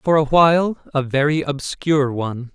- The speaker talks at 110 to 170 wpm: Yes, average, 140 wpm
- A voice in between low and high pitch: Yes, medium, 145 Hz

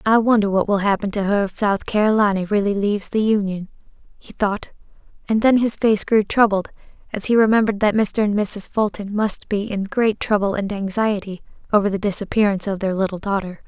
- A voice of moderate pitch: No, high, 205 Hz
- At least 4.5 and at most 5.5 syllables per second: No, 5.7 syllables/s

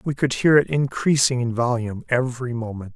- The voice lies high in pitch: No, low, 125 Hz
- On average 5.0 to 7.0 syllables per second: Yes, 5.7 syllables/s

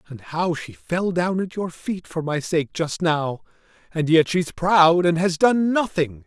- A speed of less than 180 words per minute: No, average, 200 wpm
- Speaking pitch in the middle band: Yes, medium, 170 Hz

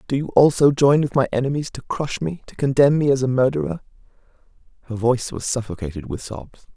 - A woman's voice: No, male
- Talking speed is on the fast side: No, average, 195 wpm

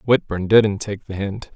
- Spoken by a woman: No, male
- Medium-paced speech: Yes, average, 195 wpm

